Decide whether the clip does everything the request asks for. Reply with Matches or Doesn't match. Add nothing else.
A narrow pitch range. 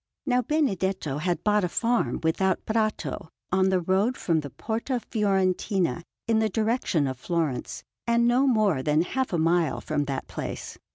Doesn't match